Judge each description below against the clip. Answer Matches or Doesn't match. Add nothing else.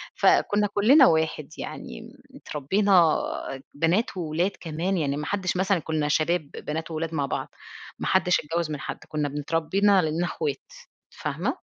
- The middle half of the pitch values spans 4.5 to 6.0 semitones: Doesn't match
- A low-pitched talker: Doesn't match